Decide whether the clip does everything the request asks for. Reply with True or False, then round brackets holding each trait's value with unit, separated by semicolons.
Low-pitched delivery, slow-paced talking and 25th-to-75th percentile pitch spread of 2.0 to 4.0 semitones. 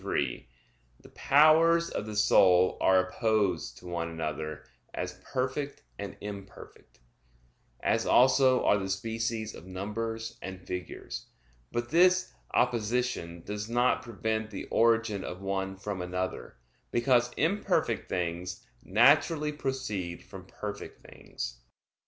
False (105 Hz; 120 wpm; 5.1 semitones)